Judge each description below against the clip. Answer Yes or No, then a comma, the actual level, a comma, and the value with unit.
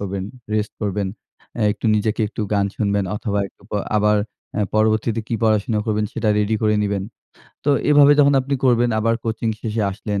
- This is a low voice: Yes, low, 110 Hz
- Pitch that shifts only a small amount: Yes, narrow, 1.9 semitones